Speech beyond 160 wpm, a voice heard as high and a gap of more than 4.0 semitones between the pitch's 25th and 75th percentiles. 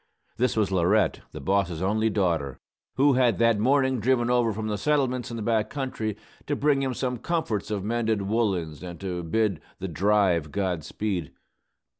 No: average, 175 wpm; low, 110 Hz; average, 4.6 semitones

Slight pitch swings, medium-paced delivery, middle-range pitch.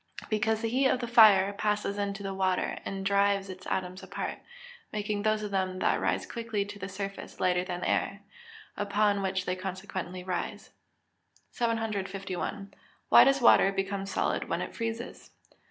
No: narrow, 2.1 semitones; average, 170 wpm; high, 200 Hz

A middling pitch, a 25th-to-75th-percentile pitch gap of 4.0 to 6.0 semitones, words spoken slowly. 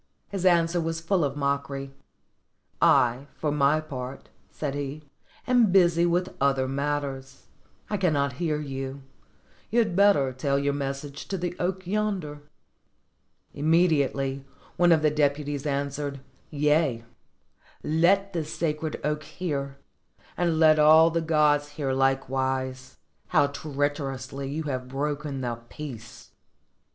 No: medium, 145 Hz; average, 3.1 semitones; slow, 125 wpm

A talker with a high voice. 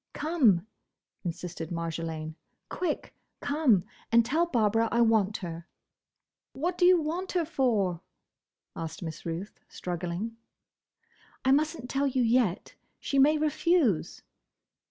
Yes: high, 230 Hz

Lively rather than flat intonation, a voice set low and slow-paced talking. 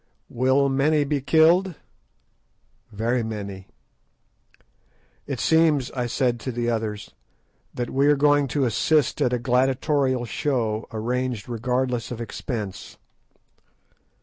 No: average, 3.3 semitones; low, 125 Hz; slow, 115 wpm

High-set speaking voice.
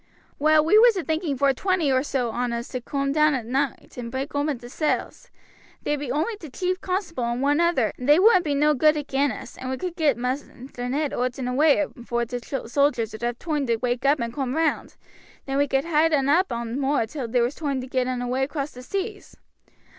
Yes: very high, 275 Hz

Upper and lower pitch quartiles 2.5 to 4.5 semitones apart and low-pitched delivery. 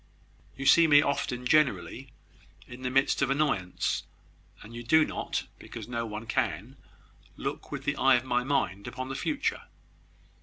Yes: average, 2.8 semitones; low, 130 Hz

